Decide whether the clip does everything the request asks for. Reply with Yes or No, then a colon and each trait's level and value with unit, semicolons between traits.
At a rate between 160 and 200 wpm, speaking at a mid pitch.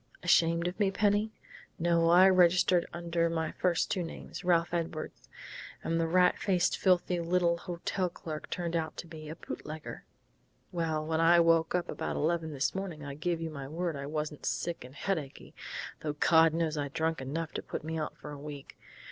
Yes: average, 190 wpm; medium, 165 Hz